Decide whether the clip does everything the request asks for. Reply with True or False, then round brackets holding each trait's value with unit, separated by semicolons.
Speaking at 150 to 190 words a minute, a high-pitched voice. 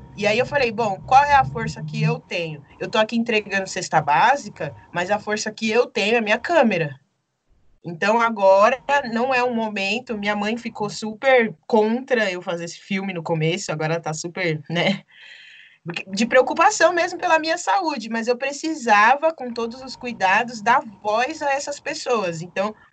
True (180 wpm; 220 Hz)